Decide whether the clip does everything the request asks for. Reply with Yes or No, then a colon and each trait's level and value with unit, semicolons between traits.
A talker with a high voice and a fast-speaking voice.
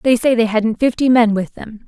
Yes: high, 230 Hz; fast, 255 wpm